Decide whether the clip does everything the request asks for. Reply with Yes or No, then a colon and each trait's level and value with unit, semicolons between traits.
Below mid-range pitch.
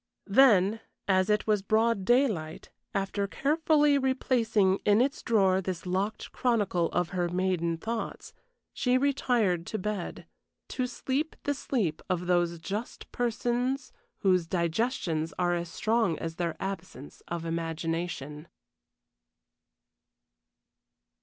No: high, 195 Hz